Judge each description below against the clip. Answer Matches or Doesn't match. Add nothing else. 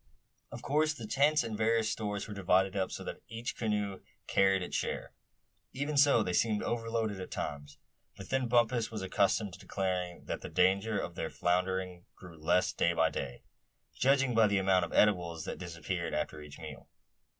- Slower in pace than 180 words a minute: Doesn't match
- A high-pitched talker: Doesn't match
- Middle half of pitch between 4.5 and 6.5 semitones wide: Doesn't match